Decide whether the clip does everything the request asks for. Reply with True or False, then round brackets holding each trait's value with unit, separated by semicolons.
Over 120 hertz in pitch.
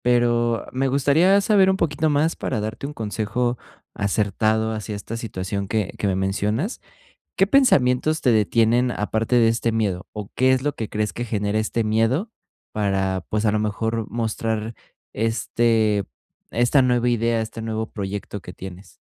False (115 Hz)